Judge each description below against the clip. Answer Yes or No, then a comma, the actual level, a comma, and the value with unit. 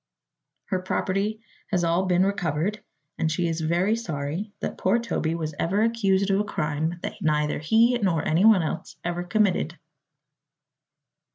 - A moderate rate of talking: Yes, average, 150 wpm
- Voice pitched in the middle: Yes, medium, 180 Hz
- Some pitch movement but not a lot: Yes, average, 4.1 semitones